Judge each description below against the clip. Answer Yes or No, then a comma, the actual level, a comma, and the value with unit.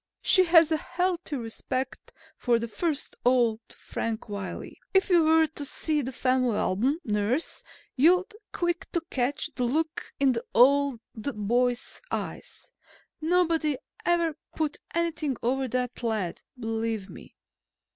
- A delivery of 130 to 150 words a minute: Yes, average, 140 wpm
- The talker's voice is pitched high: Yes, very high, 270 Hz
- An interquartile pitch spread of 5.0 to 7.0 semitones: Yes, wide, 5.5 semitones